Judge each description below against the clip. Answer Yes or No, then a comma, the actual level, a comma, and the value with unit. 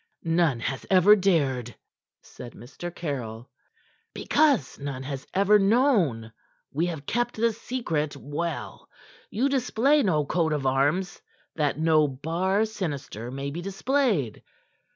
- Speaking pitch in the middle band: Yes, medium, 165 Hz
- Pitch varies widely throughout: Yes, wide, 6.7 semitones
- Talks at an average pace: No, slow, 125 wpm